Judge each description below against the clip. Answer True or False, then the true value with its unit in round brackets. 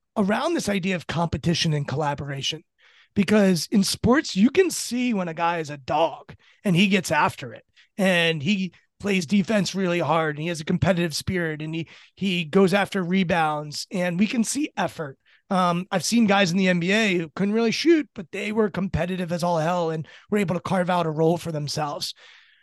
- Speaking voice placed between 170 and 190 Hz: True (185 Hz)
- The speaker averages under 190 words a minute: False (200 wpm)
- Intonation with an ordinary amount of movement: True (3.7 semitones)